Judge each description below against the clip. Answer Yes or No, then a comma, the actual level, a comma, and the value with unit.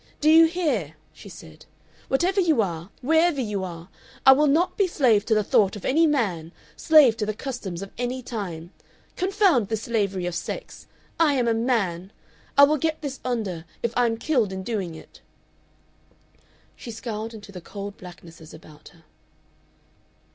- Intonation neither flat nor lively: No, wide, 7.1 semitones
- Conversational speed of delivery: Yes, average, 170 wpm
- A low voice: No, high, 225 Hz